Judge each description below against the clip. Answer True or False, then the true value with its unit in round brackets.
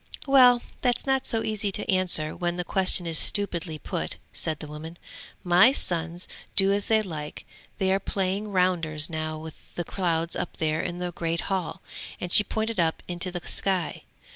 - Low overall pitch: False (180 Hz)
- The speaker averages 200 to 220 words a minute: False (180 wpm)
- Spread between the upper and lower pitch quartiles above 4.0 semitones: False (3.3 semitones)